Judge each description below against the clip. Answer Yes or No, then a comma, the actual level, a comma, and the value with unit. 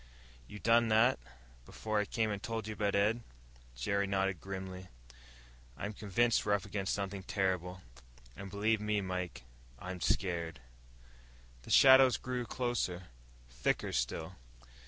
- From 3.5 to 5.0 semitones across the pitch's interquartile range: No, average, 3.0 semitones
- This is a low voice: Yes, low, 100 Hz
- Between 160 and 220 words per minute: No, slow, 135 wpm